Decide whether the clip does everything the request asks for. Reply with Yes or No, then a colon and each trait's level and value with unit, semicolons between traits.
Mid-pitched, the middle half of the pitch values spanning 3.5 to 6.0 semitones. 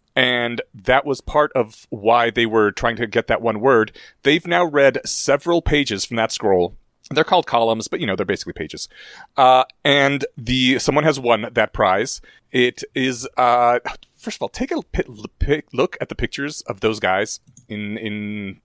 No: low, 125 Hz; average, 3.9 semitones